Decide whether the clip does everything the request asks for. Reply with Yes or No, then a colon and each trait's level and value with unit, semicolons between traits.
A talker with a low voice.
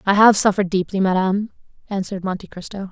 No: high, 195 Hz